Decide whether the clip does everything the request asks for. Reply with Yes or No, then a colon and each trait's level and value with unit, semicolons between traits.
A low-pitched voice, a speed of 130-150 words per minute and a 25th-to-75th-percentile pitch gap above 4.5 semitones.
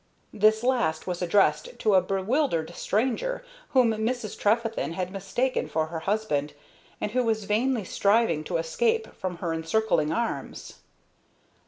No: high, 210 Hz; average, 140 wpm; average, 5.2 semitones